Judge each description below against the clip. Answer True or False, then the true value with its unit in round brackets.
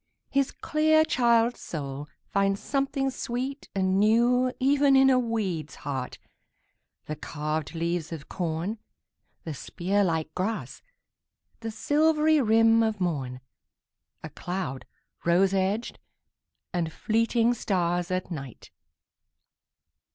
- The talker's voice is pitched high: True (200 Hz)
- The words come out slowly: True (100 wpm)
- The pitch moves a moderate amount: False (6.5 semitones)